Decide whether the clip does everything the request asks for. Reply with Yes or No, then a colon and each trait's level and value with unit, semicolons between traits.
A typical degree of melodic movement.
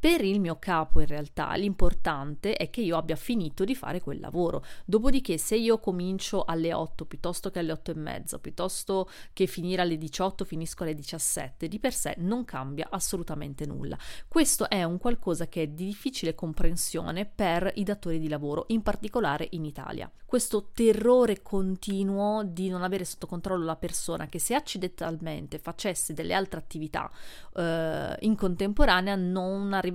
Yes: average, 3.7 semitones